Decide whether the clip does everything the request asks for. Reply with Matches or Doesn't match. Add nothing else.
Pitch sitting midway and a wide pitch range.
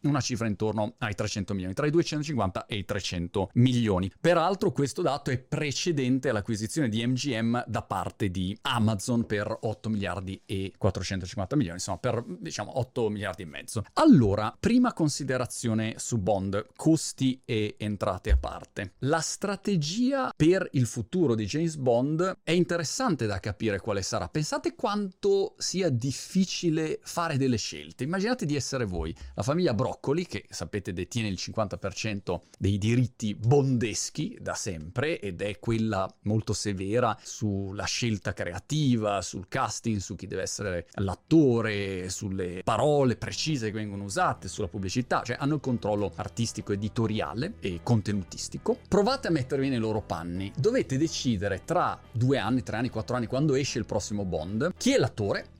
Doesn't match